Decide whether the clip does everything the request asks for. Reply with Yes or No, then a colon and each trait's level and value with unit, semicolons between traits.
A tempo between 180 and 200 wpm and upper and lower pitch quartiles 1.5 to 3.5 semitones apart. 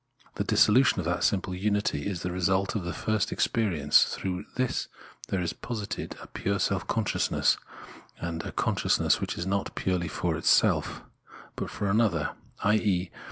No: average, 160 wpm; average, 2.9 semitones